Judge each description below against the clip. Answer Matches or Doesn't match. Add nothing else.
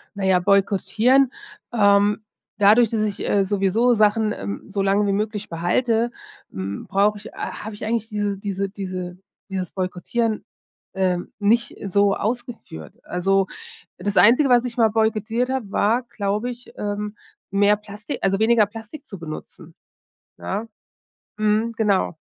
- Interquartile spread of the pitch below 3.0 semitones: Matches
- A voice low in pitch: Doesn't match